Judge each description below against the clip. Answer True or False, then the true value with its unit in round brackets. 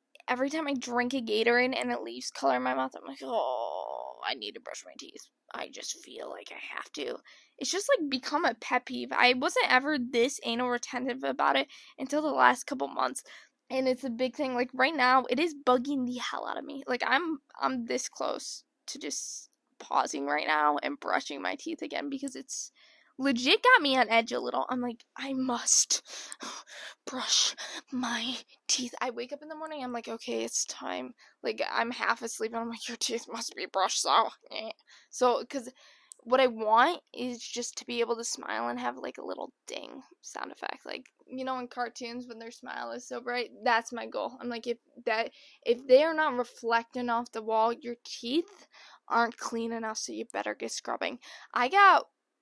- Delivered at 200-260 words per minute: True (205 wpm)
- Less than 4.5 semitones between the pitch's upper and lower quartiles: True (2.8 semitones)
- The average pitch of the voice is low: False (245 Hz)